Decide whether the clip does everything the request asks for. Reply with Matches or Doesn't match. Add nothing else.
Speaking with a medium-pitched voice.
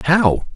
Matches